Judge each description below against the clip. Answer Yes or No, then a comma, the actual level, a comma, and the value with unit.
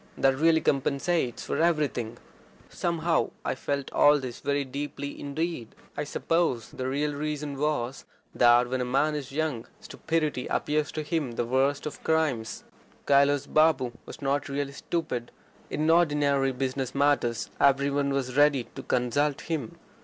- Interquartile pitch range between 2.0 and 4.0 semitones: Yes, narrow, 2.6 semitones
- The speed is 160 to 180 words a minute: No, average, 150 wpm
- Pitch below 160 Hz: Yes, medium, 140 Hz